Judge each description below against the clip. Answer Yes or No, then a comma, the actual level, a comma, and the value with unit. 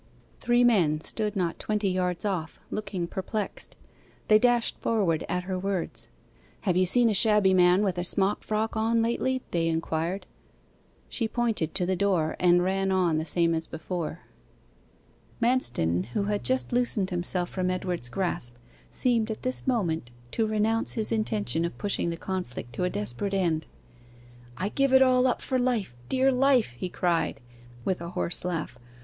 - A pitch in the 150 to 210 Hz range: Yes, high, 190 Hz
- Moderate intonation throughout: Yes, average, 4.4 semitones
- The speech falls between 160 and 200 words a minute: Yes, average, 165 wpm